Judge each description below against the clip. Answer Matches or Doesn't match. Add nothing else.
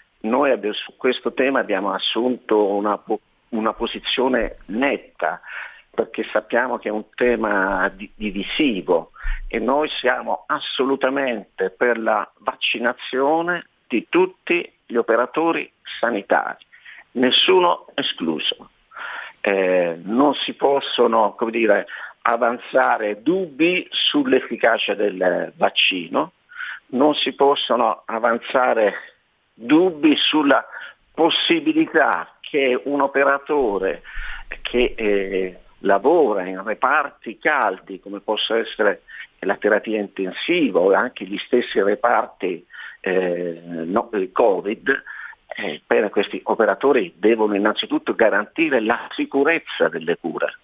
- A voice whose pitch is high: Doesn't match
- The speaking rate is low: Matches